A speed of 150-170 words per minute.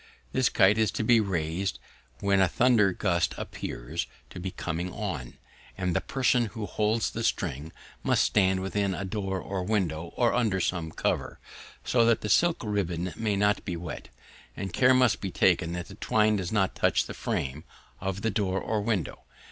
No: average, 185 wpm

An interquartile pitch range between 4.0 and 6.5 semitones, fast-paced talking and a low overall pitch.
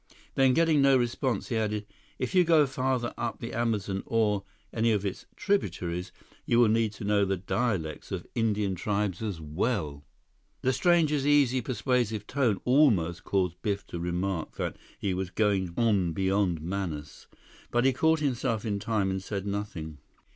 No: average, 4.7 semitones; average, 165 wpm; low, 105 Hz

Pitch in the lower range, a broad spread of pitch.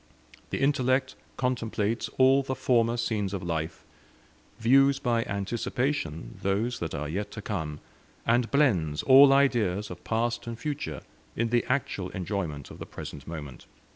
Yes: low, 115 Hz; wide, 6.5 semitones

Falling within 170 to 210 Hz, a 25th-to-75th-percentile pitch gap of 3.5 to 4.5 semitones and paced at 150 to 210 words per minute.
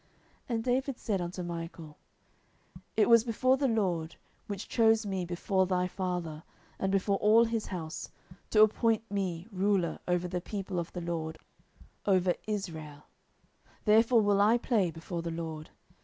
Yes: high, 190 Hz; average, 4.0 semitones; average, 155 wpm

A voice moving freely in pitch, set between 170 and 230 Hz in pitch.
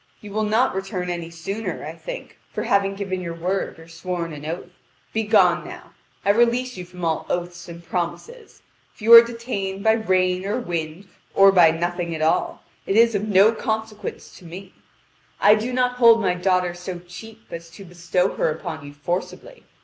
No: average, 4.1 semitones; high, 190 Hz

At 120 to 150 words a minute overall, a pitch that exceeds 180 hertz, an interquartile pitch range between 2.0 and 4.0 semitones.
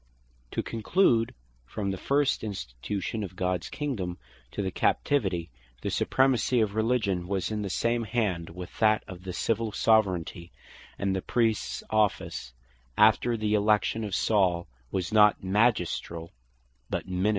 No: average, 140 wpm; low, 105 Hz; average, 3.5 semitones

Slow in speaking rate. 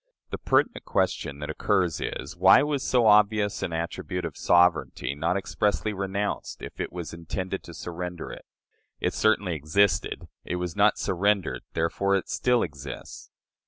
No: average, 155 wpm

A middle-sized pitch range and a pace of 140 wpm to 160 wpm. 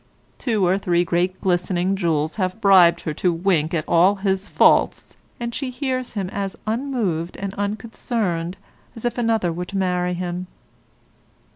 Yes: average, 3.5 semitones; average, 155 wpm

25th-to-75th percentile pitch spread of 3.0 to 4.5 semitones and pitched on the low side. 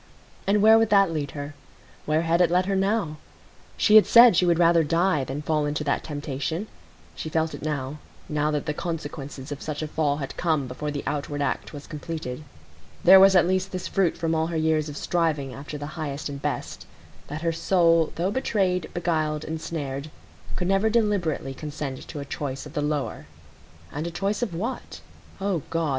No: average, 3.4 semitones; medium, 160 Hz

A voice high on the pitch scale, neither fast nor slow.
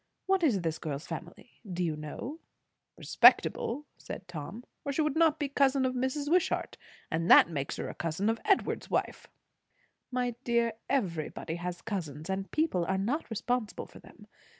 Yes: high, 225 Hz; average, 175 wpm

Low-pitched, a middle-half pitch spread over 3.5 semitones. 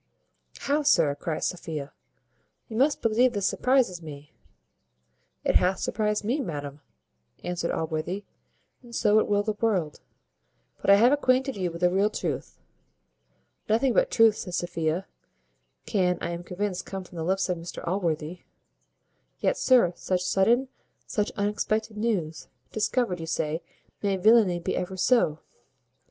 No: high, 190 Hz; average, 4.6 semitones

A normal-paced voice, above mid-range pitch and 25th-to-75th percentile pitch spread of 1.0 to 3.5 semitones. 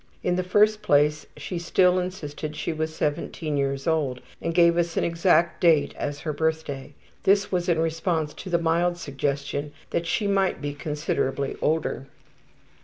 No: average, 165 wpm; medium, 160 Hz; average, 3.1 semitones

